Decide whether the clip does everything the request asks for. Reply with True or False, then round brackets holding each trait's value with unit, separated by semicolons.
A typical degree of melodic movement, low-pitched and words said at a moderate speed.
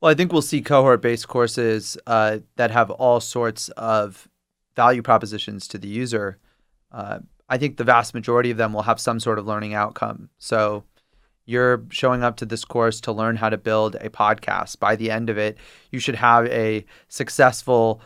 False (2.0 semitones; 115 Hz; 195 wpm)